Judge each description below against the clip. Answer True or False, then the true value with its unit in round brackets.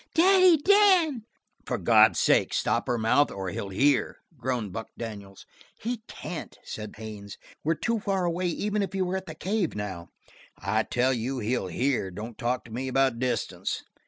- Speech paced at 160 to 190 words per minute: True (175 wpm)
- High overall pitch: False (130 Hz)